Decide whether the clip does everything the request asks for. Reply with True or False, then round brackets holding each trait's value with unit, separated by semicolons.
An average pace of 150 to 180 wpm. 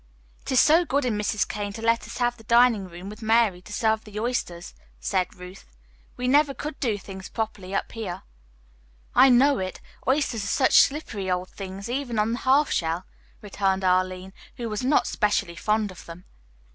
False (190 wpm)